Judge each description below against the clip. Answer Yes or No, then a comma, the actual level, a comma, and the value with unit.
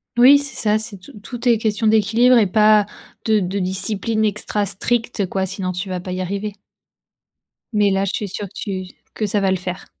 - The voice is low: No, high, 205 Hz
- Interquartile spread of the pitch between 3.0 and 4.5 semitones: No, narrow, 2.6 semitones